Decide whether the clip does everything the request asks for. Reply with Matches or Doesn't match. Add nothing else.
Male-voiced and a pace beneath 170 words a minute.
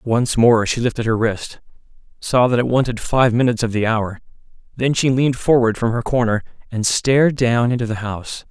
Doesn't match